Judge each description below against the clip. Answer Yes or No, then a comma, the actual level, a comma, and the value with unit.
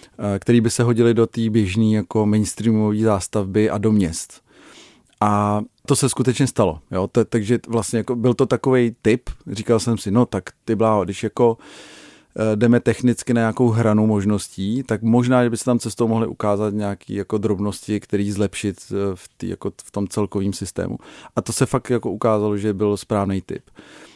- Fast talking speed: Yes, fast, 180 wpm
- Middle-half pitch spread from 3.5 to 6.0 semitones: No, narrow, 2.5 semitones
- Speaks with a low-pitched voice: Yes, low, 110 Hz